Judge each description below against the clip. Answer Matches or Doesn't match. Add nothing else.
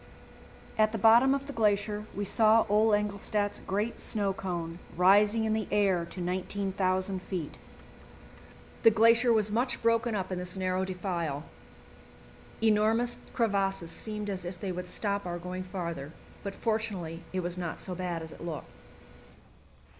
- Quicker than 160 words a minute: Doesn't match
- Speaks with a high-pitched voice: Matches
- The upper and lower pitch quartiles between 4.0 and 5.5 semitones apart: Doesn't match